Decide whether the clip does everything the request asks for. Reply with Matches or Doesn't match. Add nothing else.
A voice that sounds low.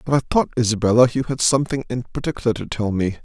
Matches